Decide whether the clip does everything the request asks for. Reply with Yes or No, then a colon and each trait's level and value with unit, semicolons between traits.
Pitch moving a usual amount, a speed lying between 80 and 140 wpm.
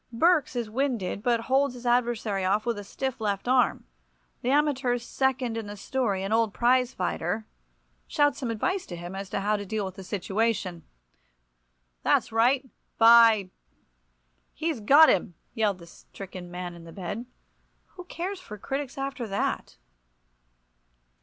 No: average, 4.9 semitones; average, 160 wpm